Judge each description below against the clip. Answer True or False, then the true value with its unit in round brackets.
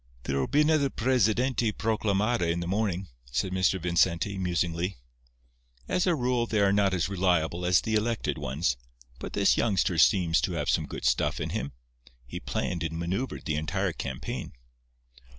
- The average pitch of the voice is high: False (95 Hz)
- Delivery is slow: False (165 wpm)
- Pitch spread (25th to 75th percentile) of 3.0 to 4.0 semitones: False (4.6 semitones)